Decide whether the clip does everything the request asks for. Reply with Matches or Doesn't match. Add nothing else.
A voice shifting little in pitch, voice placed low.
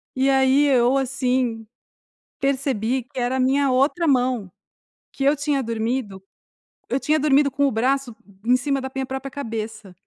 Doesn't match